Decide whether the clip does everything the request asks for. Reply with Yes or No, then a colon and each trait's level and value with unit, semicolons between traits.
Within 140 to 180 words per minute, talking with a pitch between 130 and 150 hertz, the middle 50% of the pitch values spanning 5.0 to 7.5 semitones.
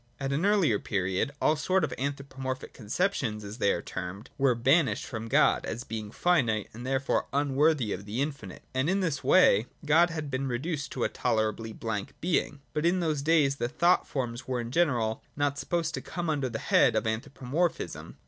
No: average, 190 wpm; low, 135 Hz; wide, 5.5 semitones